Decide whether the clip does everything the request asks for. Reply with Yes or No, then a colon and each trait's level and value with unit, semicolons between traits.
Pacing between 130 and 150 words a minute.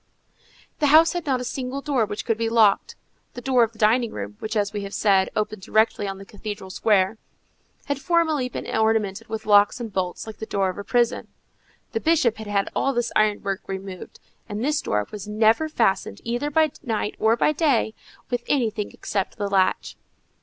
No: average, 195 wpm